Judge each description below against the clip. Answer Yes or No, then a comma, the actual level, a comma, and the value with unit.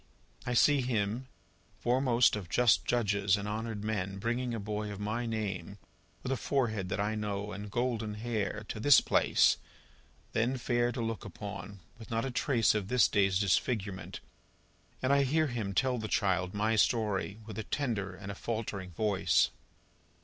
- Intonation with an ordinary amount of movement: Yes, average, 3.0 semitones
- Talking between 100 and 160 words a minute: No, average, 170 wpm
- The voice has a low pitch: Yes, low, 110 Hz